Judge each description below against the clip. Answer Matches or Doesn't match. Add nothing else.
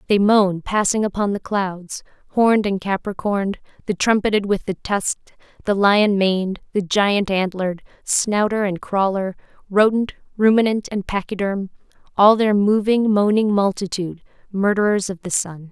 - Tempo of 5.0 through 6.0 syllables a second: Doesn't match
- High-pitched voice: Matches